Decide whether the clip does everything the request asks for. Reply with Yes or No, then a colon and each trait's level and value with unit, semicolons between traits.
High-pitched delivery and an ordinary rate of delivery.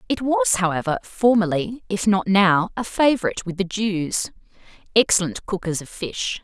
Yes: high, 195 Hz; average, 150 wpm